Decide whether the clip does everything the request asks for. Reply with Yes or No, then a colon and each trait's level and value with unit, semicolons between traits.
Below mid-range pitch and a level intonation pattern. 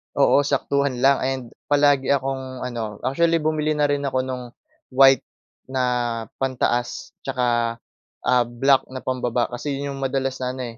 Yes: low, 130 Hz; narrow, 1.9 semitones